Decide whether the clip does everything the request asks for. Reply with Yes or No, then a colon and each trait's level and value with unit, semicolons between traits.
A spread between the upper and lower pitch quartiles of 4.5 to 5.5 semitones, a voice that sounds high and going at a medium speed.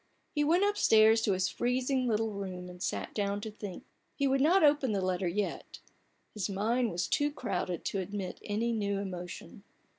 Yes: average, 4.9 semitones; high, 210 Hz; average, 180 wpm